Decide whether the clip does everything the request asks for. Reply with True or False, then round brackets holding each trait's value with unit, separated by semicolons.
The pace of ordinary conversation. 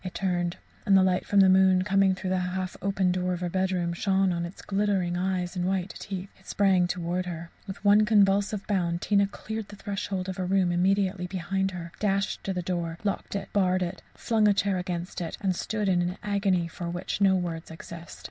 False (215 wpm)